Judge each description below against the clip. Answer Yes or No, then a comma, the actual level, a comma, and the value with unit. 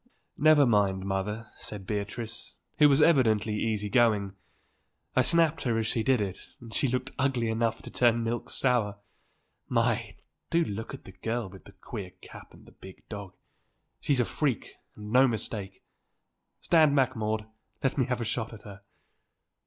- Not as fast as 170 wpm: No, average, 175 wpm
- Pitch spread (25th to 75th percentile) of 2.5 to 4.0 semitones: Yes, average, 3.6 semitones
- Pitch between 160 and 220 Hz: No, low, 115 Hz